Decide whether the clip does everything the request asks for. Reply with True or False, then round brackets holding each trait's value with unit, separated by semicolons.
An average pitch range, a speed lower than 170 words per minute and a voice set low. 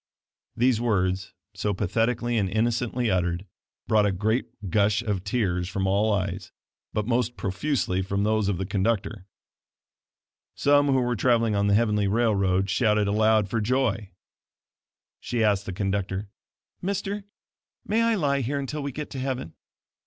True (3.8 semitones; 150 wpm; 105 Hz)